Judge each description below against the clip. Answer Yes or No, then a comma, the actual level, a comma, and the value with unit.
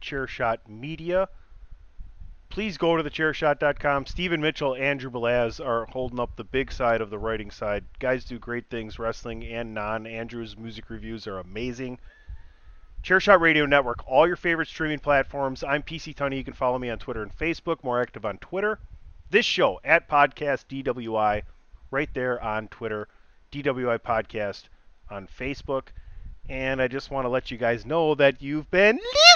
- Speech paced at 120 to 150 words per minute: No, average, 165 wpm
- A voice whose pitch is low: Yes, low, 130 Hz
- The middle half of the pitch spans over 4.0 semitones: Yes, average, 4.5 semitones